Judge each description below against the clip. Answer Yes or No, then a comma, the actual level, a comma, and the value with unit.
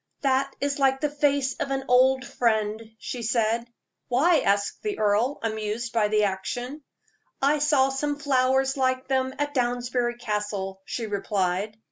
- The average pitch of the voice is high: Yes, very high, 250 Hz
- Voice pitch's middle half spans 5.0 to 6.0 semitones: No, average, 4.0 semitones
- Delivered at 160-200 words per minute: No, average, 150 wpm